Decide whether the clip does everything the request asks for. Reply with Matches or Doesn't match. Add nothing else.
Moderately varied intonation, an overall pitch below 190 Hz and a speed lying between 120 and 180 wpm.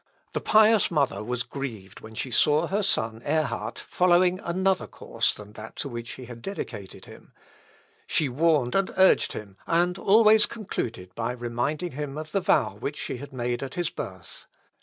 Doesn't match